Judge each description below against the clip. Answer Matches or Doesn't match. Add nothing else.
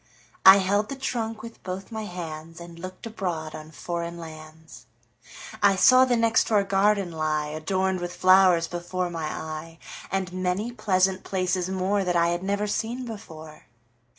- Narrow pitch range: Doesn't match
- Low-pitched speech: Doesn't match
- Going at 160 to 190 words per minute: Doesn't match